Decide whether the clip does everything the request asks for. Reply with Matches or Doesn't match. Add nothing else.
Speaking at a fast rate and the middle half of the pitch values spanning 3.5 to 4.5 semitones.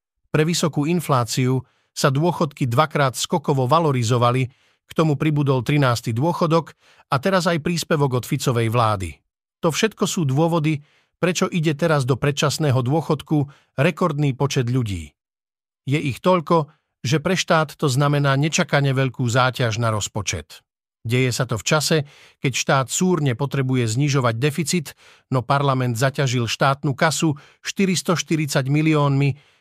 Doesn't match